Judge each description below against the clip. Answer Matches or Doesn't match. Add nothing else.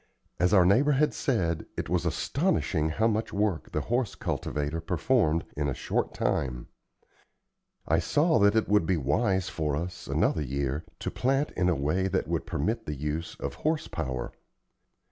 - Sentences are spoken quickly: Doesn't match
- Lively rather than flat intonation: Matches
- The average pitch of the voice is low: Matches